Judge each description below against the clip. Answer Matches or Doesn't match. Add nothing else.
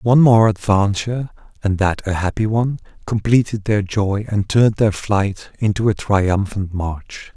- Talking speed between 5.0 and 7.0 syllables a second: Doesn't match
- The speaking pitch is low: Matches